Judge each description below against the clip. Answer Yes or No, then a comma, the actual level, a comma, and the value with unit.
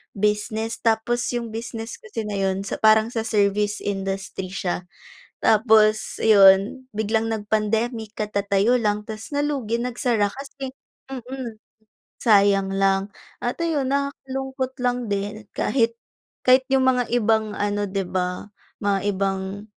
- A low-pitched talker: No, high, 220 Hz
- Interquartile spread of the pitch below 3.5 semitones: Yes, average, 3.1 semitones